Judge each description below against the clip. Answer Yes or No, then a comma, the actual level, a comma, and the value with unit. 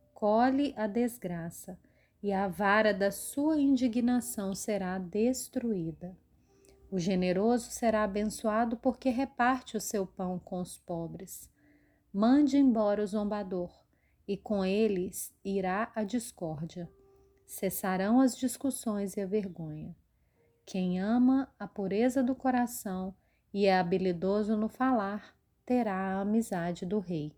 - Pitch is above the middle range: Yes, high, 205 Hz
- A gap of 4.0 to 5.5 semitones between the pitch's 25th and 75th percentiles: Yes, average, 4.4 semitones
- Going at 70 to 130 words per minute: Yes, slow, 120 wpm